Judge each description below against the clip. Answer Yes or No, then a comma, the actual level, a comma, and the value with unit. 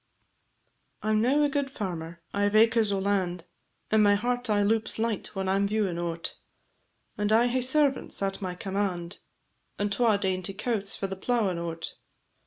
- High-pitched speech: Yes, high, 205 Hz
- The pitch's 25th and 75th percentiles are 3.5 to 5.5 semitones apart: No, average, 3.1 semitones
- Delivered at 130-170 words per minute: No, average, 185 wpm